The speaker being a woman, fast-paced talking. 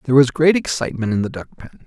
No: male; fast, 260 wpm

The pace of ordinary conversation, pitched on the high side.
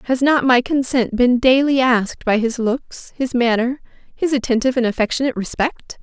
Yes: average, 170 wpm; very high, 250 Hz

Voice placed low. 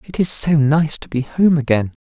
No: medium, 150 Hz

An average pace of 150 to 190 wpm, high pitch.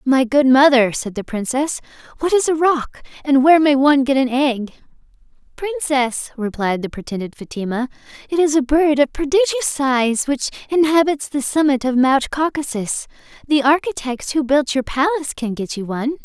Yes: average, 170 wpm; very high, 275 Hz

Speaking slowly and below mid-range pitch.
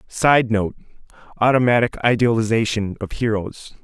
Yes: slow, 80 wpm; low, 115 Hz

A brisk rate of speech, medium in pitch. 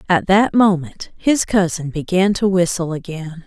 No: average, 155 wpm; medium, 180 Hz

